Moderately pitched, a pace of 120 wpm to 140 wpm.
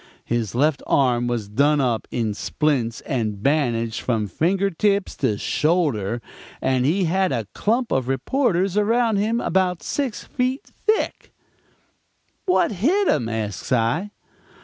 Yes: medium, 145 Hz; slow, 135 wpm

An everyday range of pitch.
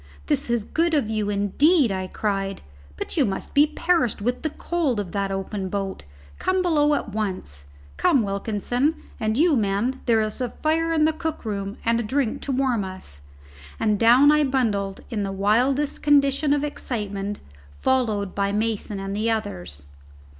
No: wide, 6.0 semitones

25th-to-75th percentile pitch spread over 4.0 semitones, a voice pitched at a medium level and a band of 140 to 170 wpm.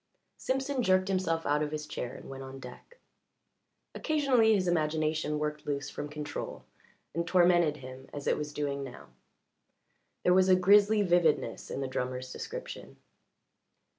Yes: average, 4.5 semitones; medium, 155 Hz; average, 150 wpm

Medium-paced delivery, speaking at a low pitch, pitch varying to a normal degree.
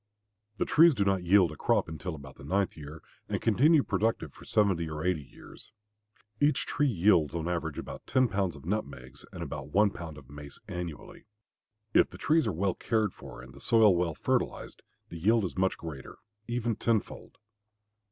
No: average, 190 wpm; very low, 90 Hz; wide, 5.7 semitones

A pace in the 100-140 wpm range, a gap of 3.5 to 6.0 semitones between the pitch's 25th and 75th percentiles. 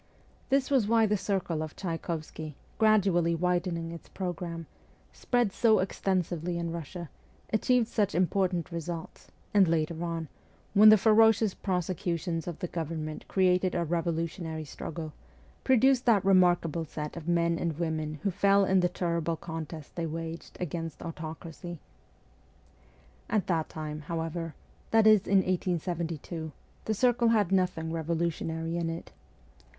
No: slow, 135 wpm; average, 2.9 semitones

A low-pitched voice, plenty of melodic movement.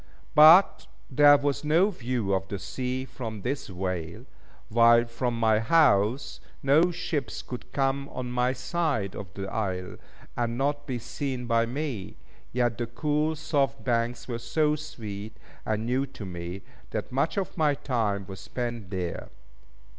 No: low, 120 Hz; average, 4.8 semitones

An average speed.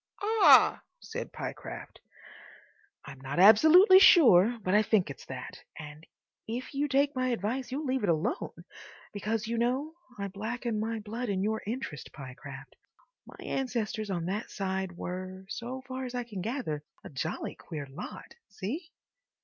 Yes: average, 150 wpm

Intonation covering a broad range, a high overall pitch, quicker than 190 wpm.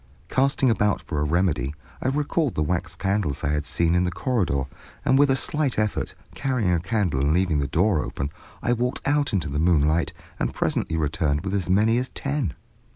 No: wide, 8.0 semitones; very low, 90 Hz; average, 200 wpm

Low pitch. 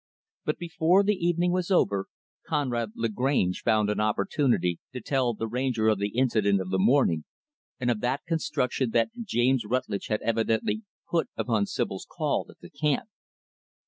Yes: low, 120 Hz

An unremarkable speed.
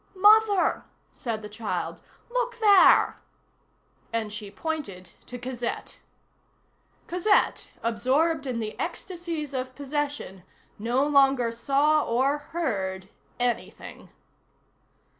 No: slow, 95 wpm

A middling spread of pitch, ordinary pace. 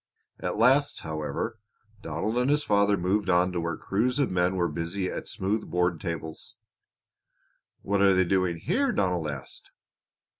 Yes: average, 4.0 semitones; average, 155 wpm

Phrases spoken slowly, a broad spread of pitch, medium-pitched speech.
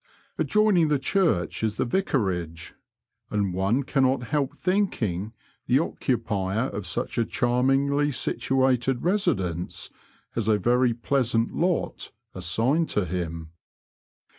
No: slow, 115 wpm; wide, 6.0 semitones; low, 120 Hz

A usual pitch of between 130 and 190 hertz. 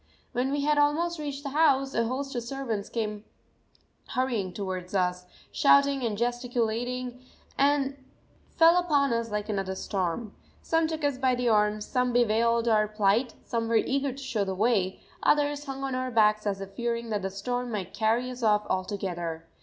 No: high, 235 Hz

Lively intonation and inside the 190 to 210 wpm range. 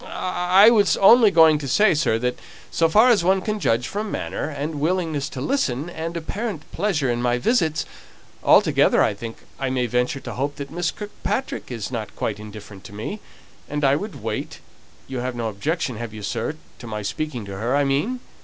Yes: wide, 7.0 semitones; average, 200 wpm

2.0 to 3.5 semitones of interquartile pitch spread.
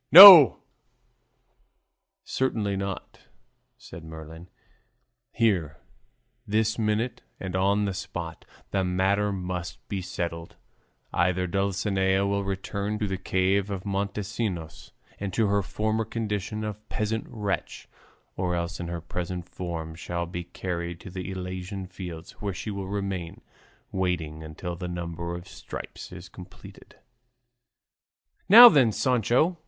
Yes: average, 2.9 semitones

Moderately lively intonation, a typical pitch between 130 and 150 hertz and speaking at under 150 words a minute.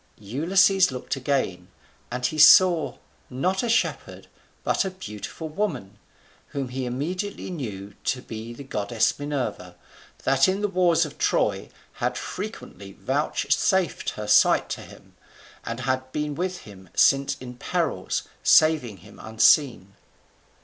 No: wide, 7.0 semitones; low, 135 Hz; slow, 135 wpm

